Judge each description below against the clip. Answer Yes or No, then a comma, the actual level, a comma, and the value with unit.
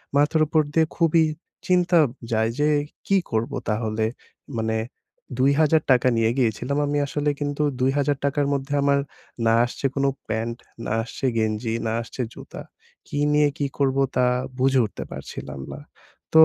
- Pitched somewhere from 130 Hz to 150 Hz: Yes, low, 135 Hz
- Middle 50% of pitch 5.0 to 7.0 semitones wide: No, average, 4.3 semitones